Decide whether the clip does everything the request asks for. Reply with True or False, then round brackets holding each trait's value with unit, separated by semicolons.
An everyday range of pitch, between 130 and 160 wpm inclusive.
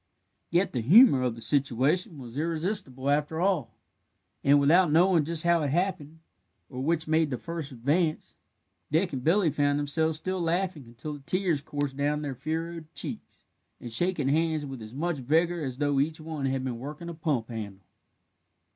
False (3.6 semitones; 175 wpm)